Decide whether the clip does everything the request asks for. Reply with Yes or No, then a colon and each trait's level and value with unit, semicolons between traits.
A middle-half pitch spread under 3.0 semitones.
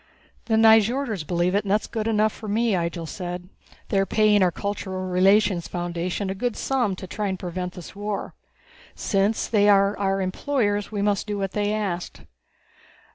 Yes: narrow, 2.5 semitones